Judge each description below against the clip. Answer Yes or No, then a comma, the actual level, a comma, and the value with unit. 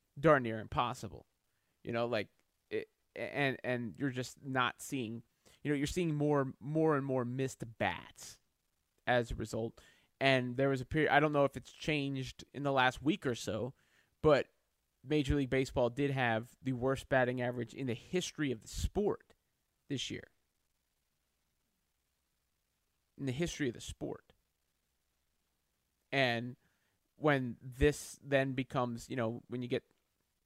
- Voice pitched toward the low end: Yes, low, 130 Hz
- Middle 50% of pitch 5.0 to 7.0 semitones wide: No, average, 3.6 semitones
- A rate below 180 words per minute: Yes, average, 150 wpm